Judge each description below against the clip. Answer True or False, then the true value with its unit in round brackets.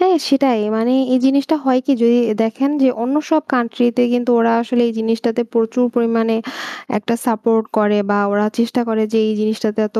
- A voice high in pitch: True (235 Hz)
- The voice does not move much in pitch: True (2.1 semitones)